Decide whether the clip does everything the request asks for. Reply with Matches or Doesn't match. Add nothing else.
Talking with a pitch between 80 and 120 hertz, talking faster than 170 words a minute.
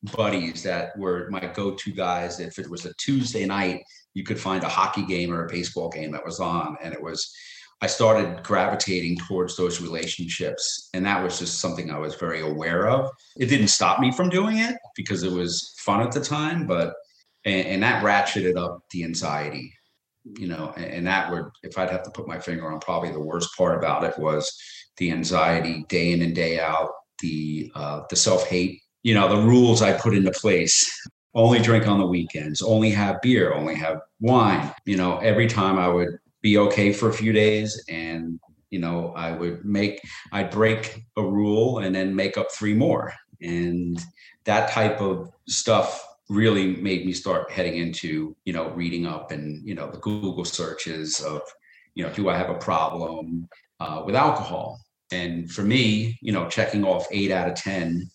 Matches